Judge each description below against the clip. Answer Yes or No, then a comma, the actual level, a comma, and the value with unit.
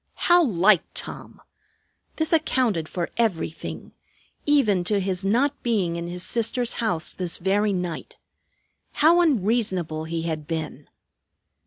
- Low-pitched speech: No, high, 195 Hz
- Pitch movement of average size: No, wide, 6.0 semitones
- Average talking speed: No, slow, 125 wpm